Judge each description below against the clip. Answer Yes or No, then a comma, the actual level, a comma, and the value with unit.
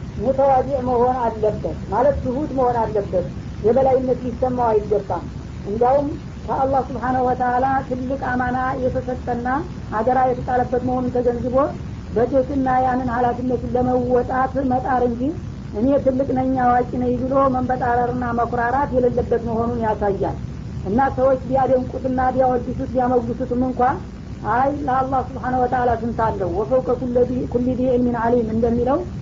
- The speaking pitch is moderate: No, very high, 250 Hz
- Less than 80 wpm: No, fast, 110 wpm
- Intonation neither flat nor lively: No, narrow, 1.1 semitones